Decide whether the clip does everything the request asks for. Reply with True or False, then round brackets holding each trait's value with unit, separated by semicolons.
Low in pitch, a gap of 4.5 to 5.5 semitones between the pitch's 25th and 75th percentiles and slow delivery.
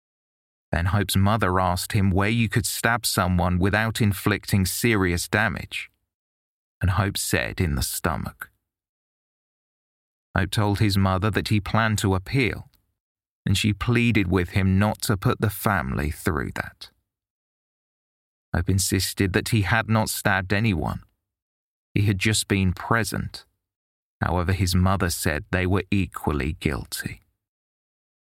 False (100 Hz; 2.4 semitones; 130 wpm)